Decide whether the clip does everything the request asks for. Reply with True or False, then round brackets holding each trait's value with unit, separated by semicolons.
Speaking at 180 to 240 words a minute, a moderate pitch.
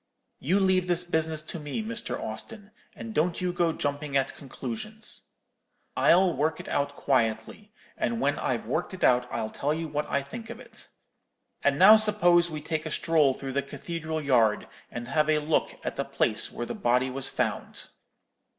True (185 wpm; 155 Hz)